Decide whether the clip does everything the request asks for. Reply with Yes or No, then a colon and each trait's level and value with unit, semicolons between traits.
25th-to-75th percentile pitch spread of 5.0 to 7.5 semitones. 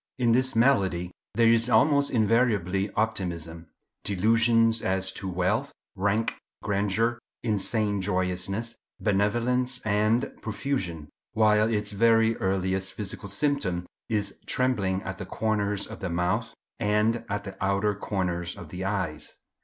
No: average, 3.3 semitones